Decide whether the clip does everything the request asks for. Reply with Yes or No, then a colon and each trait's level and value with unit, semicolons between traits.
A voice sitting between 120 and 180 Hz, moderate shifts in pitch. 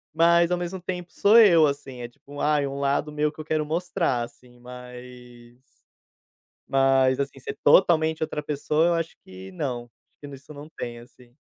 Yes: medium, 140 Hz; average, 4.4 semitones